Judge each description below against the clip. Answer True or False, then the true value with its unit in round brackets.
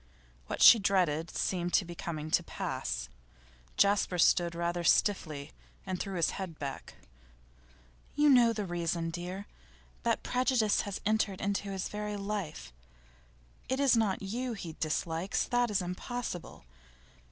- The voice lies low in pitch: False (190 Hz)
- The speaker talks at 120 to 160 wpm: True (140 wpm)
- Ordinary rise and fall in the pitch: True (3.7 semitones)